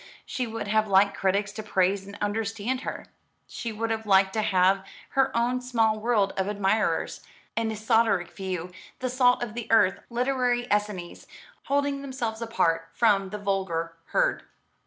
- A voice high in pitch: Yes, high, 215 Hz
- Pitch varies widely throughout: No, average, 3.5 semitones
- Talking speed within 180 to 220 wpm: No, average, 155 wpm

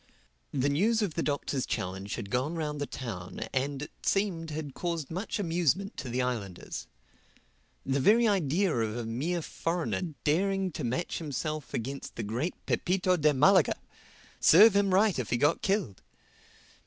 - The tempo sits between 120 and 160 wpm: Yes, average, 155 wpm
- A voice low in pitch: No, medium, 150 Hz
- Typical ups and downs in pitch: No, wide, 6.2 semitones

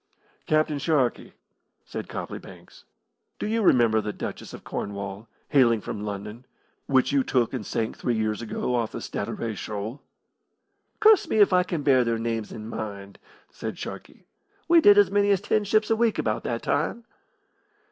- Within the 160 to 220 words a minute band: Yes, average, 170 wpm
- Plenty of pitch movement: Yes, wide, 9.0 semitones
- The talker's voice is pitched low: Yes, low, 125 Hz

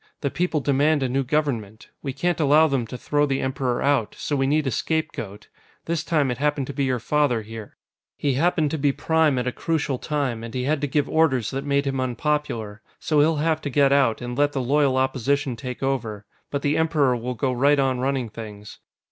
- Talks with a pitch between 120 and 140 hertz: Yes, low, 135 Hz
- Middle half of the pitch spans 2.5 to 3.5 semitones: Yes, average, 2.9 semitones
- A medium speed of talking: No, fast, 220 wpm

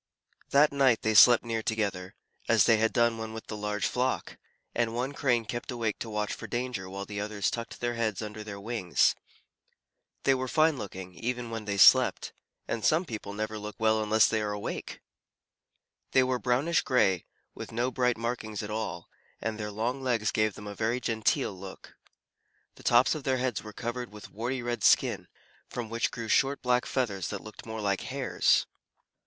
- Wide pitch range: No, average, 2.7 semitones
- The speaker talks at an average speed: Yes, average, 190 wpm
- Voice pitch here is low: Yes, low, 115 Hz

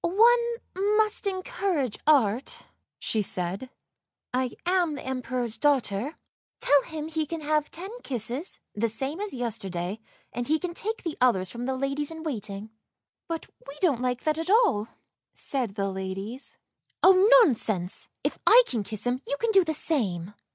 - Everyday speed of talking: Yes, average, 170 wpm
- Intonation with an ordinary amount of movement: No, wide, 7.3 semitones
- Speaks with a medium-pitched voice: No, very high, 275 Hz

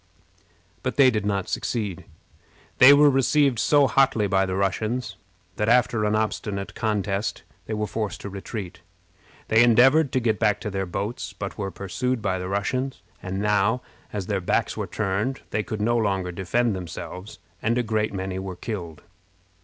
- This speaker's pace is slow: No, average, 170 wpm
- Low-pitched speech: Yes, low, 105 Hz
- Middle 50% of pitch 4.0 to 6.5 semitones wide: No, average, 3.6 semitones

